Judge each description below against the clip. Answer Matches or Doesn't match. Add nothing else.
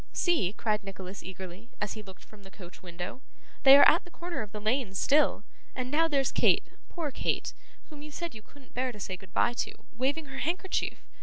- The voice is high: Matches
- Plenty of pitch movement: Matches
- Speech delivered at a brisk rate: Matches